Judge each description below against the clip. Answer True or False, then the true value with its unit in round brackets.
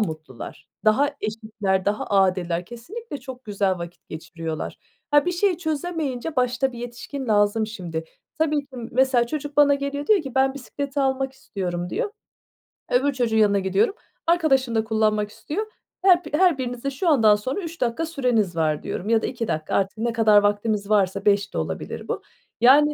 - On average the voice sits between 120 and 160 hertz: False (240 Hz)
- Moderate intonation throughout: False (5.7 semitones)